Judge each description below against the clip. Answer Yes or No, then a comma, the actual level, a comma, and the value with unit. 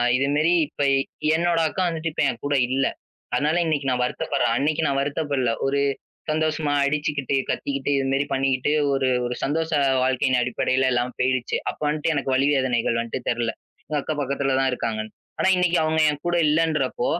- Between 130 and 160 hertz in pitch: Yes, medium, 140 Hz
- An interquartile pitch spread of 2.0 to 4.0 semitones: Yes, average, 3.0 semitones